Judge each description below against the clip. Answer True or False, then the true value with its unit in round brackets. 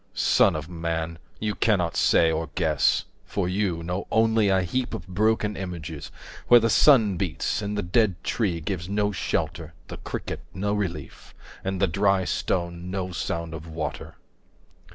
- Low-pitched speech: True (90 Hz)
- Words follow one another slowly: False (165 wpm)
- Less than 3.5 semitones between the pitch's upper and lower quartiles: False (3.8 semitones)